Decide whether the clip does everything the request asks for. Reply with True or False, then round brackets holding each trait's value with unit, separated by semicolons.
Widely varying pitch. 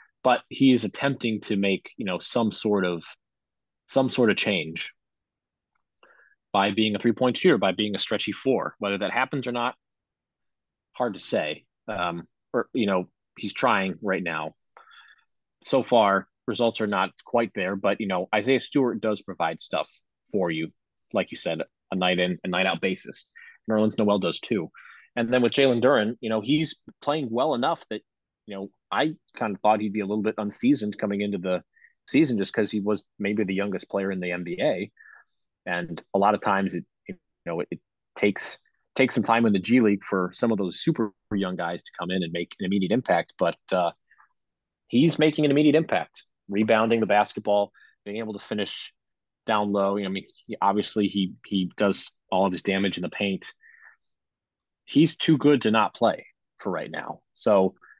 False (3.4 semitones)